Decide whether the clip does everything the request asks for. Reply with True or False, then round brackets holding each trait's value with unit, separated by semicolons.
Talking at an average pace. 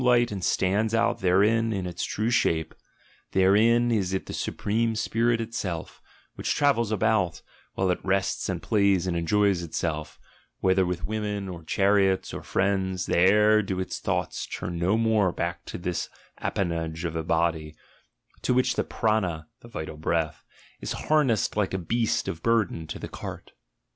True (165 wpm)